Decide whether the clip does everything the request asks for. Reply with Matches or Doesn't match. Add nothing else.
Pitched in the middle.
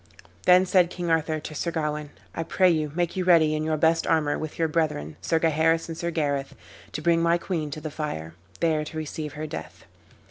Matches